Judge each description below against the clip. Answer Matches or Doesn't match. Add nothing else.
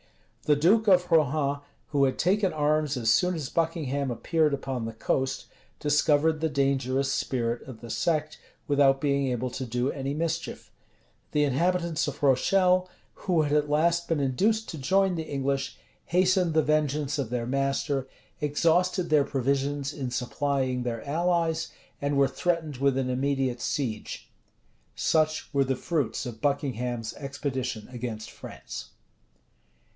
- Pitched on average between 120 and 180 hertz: Matches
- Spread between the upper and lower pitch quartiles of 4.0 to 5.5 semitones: Doesn't match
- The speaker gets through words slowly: Doesn't match